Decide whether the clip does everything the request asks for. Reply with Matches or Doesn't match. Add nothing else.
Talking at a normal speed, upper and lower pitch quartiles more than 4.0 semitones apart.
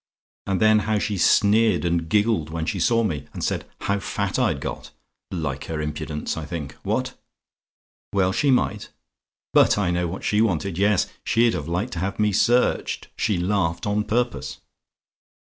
Matches